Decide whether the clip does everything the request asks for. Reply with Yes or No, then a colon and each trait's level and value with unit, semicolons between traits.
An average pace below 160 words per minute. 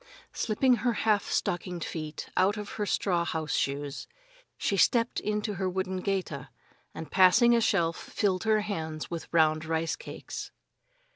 Yes: average, 150 wpm